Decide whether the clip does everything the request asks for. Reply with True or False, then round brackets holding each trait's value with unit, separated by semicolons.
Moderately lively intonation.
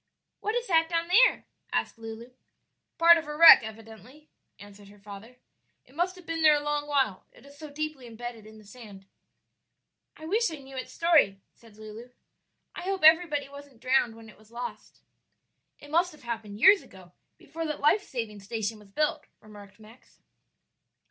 False (6.4 semitones)